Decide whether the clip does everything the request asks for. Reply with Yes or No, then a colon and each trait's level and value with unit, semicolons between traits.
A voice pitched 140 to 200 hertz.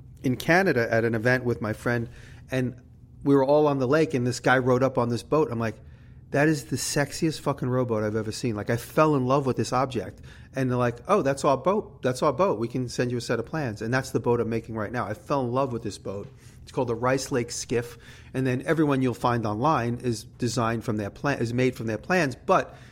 No: low, 125 Hz